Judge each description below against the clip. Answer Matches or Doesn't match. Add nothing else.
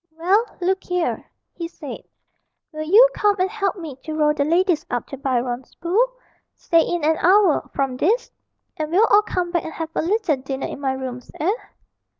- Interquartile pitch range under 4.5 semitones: Doesn't match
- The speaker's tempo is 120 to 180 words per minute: Doesn't match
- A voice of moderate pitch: Doesn't match